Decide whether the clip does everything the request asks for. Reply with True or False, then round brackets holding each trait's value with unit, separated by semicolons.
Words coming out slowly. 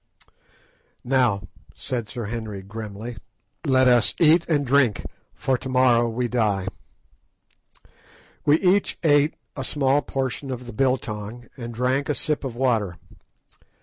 True (130 wpm)